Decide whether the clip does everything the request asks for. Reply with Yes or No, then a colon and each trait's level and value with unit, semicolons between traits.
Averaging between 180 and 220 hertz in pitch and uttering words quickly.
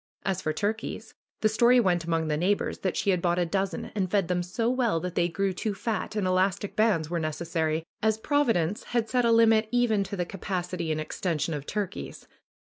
Yes: high, 190 Hz; fast, 210 wpm